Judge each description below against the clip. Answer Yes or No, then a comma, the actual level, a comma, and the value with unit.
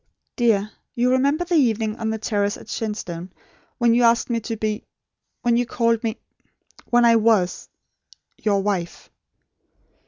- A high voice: Yes, high, 225 Hz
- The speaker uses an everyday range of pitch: No, narrow, 2.2 semitones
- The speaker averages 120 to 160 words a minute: Yes, average, 150 wpm